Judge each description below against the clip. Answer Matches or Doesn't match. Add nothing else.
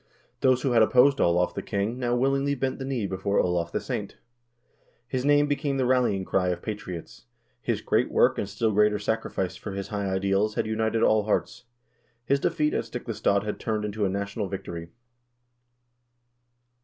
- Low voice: Matches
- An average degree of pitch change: Matches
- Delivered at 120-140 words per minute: Doesn't match